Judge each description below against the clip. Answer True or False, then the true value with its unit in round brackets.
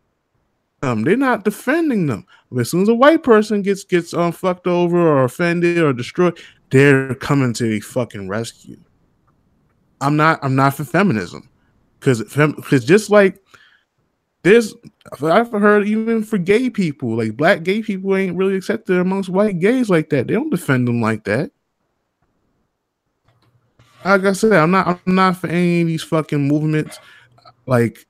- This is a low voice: False (170 Hz)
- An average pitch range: False (6.8 semitones)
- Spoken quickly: False (160 wpm)